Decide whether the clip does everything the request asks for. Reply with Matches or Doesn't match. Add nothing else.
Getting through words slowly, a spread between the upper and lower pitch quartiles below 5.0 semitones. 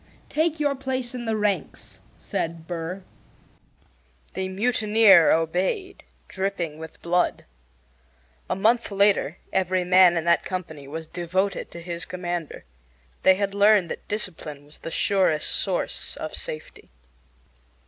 Matches